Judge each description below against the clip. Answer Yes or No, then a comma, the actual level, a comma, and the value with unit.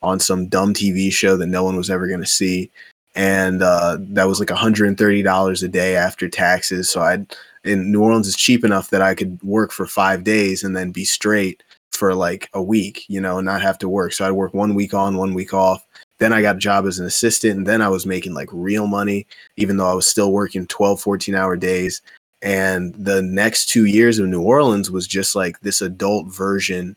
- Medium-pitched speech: No, very low, 95 Hz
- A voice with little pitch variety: Yes, narrow, 1.4 semitones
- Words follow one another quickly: Yes, fast, 230 wpm